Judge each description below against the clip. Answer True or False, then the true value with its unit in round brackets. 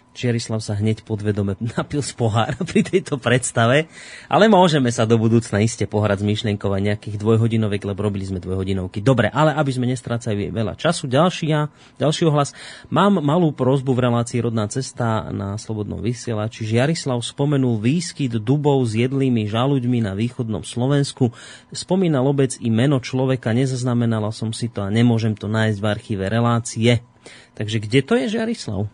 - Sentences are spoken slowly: False (165 wpm)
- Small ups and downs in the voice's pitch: False (4.1 semitones)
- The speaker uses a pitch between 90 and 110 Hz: False (120 Hz)